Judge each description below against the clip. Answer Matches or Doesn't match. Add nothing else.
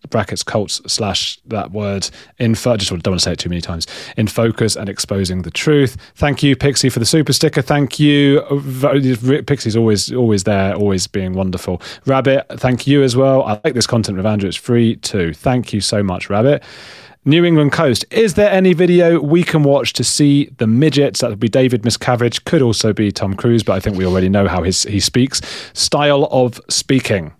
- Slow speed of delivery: Doesn't match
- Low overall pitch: Matches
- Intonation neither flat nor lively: Doesn't match